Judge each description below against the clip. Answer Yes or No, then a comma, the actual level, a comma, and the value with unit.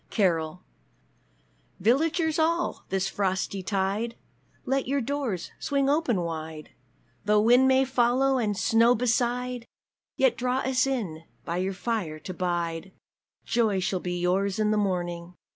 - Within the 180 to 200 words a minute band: No, average, 140 wpm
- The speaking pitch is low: No, high, 215 Hz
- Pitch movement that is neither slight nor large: No, wide, 5.7 semitones